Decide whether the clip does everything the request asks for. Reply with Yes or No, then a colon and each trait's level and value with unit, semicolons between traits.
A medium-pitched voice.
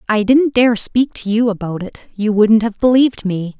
No: high, 220 Hz